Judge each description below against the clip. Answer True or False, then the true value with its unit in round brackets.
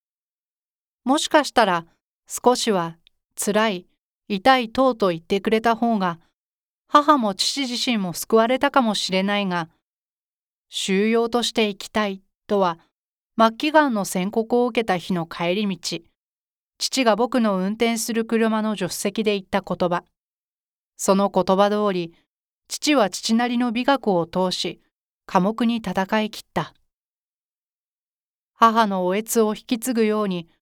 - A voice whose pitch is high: True (215 Hz)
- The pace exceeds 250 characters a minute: False (240 characters per minute)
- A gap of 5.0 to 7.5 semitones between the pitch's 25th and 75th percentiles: False (3.9 semitones)